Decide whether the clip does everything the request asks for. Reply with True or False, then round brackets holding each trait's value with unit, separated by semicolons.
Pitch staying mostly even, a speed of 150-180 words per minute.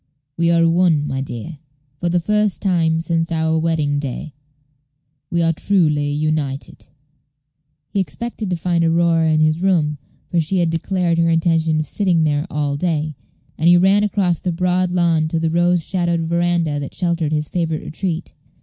True (2.1 semitones; 175 wpm)